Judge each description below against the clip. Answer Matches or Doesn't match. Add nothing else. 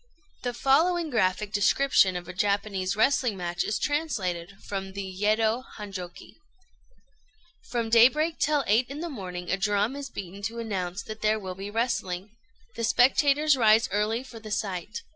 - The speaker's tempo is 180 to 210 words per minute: Doesn't match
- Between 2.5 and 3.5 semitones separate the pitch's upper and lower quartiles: Doesn't match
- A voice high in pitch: Matches